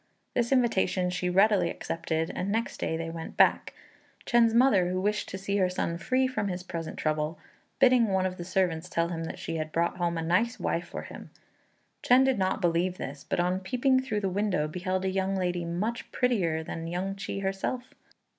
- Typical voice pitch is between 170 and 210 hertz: Yes, medium, 185 Hz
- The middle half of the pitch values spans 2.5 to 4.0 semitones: Yes, average, 3.7 semitones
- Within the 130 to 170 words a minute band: No, fast, 205 wpm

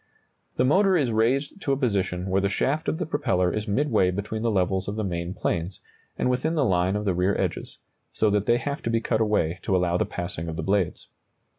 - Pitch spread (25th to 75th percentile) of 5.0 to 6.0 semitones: Yes, wide, 5.5 semitones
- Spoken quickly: Yes, fast, 240 wpm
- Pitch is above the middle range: No, low, 105 Hz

